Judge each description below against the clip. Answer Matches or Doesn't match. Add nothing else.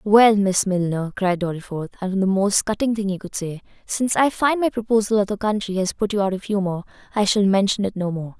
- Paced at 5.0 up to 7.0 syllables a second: Doesn't match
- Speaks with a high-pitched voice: Matches